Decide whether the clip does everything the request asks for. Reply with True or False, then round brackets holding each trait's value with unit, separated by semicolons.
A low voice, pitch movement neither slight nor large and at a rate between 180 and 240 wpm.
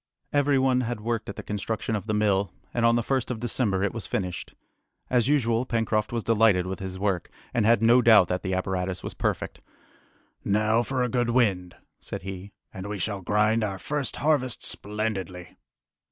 True (110 Hz; 3.7 semitones; 190 wpm)